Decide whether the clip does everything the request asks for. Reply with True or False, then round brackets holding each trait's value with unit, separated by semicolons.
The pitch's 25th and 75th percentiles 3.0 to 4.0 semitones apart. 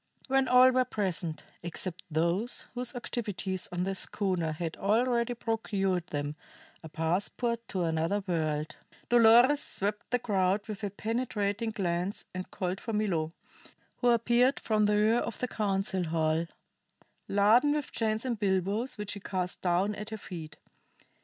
False (4.5 semitones)